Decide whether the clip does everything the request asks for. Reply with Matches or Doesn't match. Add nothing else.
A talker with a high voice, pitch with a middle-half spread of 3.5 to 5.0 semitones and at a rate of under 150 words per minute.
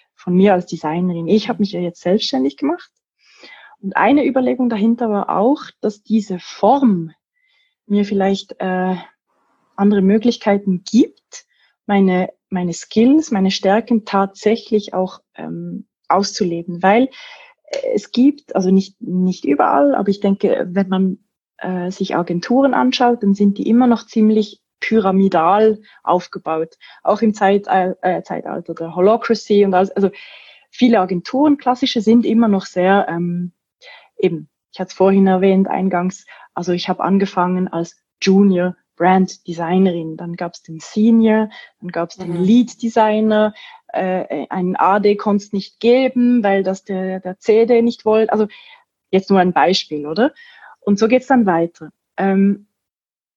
Matches